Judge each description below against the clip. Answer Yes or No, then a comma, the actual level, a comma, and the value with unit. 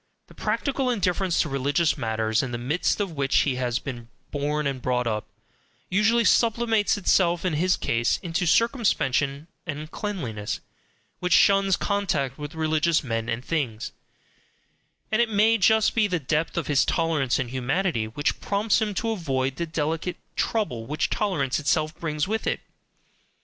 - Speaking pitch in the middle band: Yes, medium, 155 Hz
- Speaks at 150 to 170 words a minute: Yes, average, 160 wpm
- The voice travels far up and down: Yes, wide, 6.8 semitones